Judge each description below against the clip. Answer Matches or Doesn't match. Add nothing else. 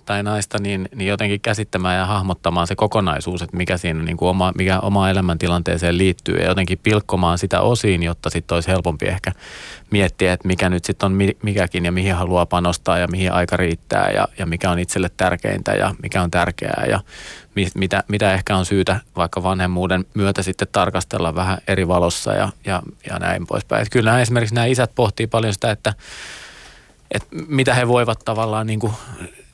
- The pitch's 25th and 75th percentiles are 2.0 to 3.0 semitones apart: Matches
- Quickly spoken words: Matches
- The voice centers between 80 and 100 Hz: Matches